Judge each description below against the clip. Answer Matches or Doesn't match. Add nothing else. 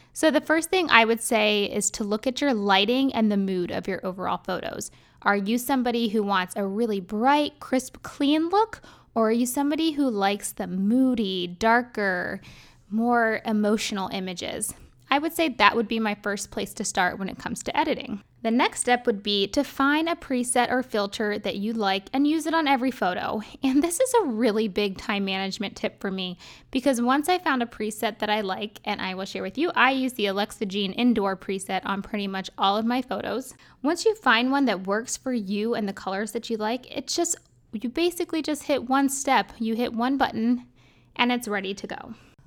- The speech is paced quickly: Matches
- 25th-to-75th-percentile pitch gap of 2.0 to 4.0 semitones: Doesn't match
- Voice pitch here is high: Matches